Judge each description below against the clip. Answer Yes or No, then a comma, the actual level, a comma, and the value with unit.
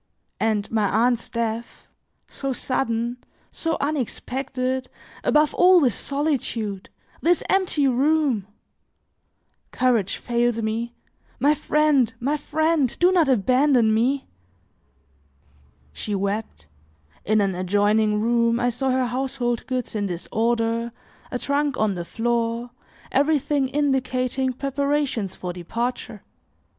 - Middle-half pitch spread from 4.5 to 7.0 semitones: No, average, 3.8 semitones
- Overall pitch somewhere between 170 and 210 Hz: No, high, 245 Hz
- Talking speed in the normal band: No, slow, 110 wpm